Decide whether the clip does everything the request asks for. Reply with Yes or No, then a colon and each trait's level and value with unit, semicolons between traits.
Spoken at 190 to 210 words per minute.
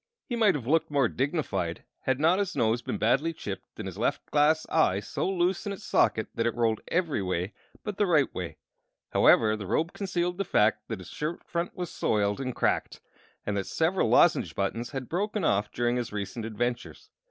Yes: average, 200 wpm